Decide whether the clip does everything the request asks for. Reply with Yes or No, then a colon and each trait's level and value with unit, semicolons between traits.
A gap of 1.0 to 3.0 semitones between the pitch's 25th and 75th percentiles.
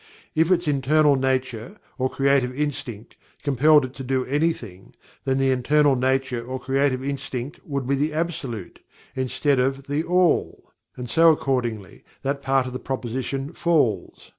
Yes: narrow, 2.4 semitones